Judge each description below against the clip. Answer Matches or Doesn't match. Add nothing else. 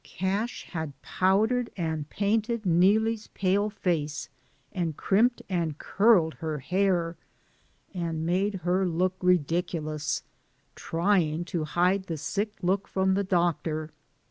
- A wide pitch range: Doesn't match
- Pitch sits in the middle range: Matches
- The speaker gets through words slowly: Matches